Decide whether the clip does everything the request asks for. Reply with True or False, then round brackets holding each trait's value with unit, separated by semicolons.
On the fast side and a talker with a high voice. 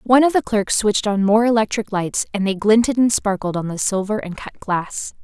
True (230 wpm; 210 Hz)